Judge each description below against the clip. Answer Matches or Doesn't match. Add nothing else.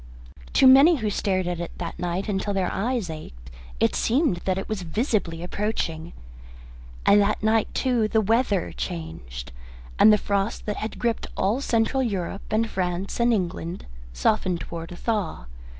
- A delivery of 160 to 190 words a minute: Matches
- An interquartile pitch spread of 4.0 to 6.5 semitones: Matches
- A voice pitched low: Doesn't match